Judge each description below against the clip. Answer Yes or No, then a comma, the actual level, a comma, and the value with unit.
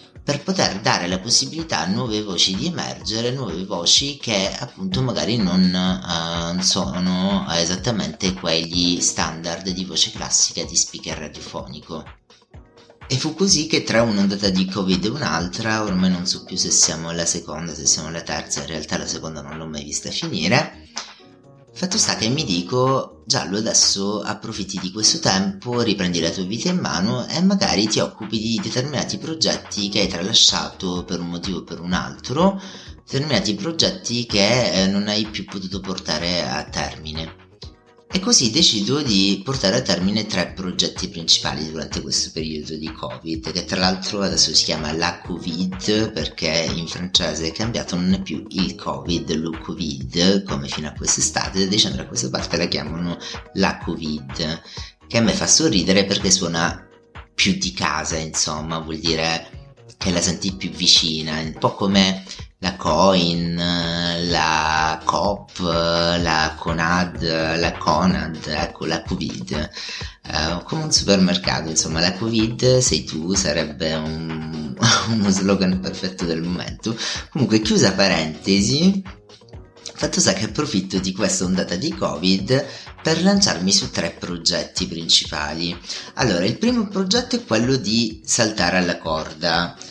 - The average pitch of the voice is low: Yes, very low, 95 Hz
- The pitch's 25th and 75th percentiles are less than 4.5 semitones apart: No, average, 4.8 semitones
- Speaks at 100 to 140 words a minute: No, average, 150 wpm